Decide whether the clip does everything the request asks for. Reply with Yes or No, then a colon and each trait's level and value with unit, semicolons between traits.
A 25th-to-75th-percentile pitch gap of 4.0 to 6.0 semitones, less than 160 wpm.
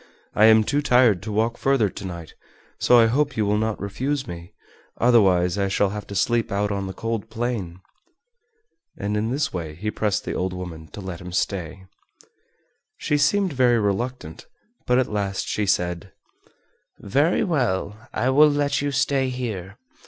No: average, 4.7 semitones; average, 175 wpm